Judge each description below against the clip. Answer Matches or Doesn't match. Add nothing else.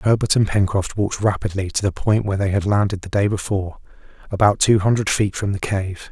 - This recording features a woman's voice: Doesn't match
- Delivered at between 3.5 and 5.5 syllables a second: Doesn't match